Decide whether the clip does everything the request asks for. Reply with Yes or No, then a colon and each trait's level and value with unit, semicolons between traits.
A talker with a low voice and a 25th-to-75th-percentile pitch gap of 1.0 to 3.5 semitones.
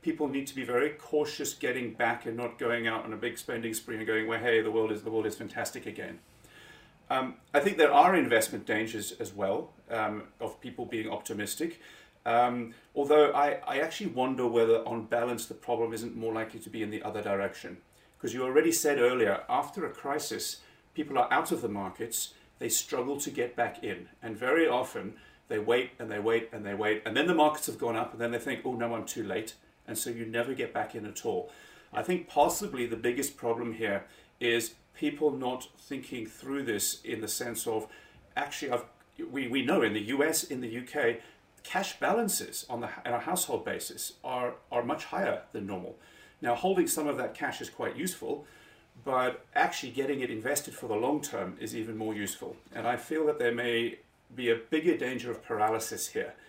No: low, 120 Hz; average, 4.0 semitones